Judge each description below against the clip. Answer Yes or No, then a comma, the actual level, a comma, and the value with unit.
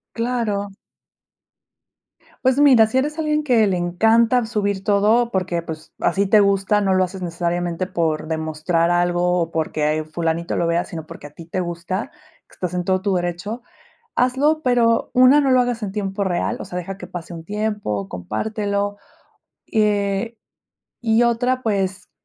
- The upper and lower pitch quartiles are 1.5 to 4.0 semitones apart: No, average, 4.7 semitones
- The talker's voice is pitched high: Yes, high, 195 Hz